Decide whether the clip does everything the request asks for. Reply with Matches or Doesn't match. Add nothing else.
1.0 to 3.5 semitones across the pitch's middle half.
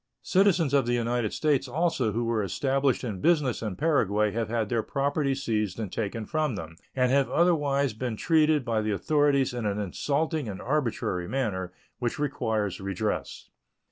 Doesn't match